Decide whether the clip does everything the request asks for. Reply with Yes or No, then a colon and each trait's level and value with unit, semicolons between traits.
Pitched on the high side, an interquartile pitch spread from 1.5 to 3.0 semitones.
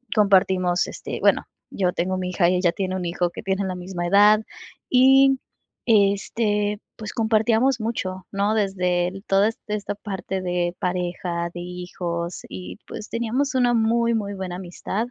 No: high, 195 Hz; average, 3.4 semitones